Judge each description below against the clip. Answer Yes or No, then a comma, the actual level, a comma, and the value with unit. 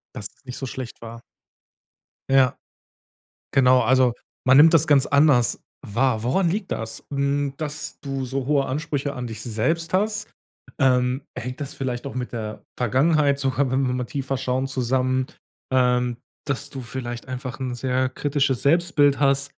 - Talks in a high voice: No, low, 130 Hz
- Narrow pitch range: Yes, narrow, 2.1 semitones